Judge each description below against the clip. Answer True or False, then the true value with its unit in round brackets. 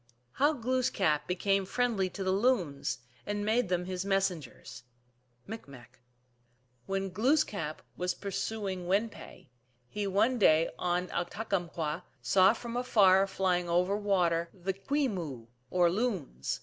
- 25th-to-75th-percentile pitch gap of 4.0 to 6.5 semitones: False (3.4 semitones)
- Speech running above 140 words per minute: False (135 wpm)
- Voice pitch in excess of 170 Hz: True (190 Hz)